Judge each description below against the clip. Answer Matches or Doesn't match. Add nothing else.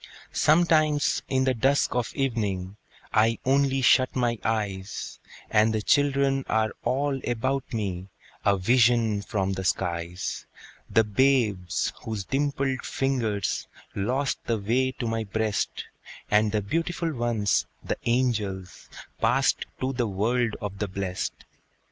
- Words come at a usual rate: Doesn't match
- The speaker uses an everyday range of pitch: Matches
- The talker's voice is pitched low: Matches